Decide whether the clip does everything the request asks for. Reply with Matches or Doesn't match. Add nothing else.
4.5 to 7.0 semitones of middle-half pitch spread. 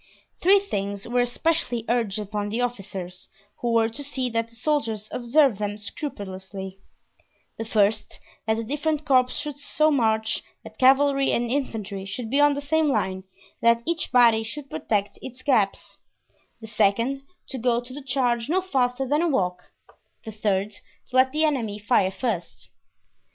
Matches